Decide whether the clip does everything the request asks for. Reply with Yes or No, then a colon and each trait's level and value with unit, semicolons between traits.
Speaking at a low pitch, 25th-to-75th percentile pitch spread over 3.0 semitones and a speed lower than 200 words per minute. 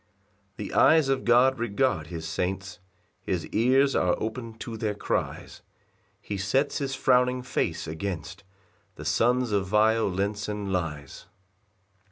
Yes: low, 105 Hz; average, 4.7 semitones; slow, 135 wpm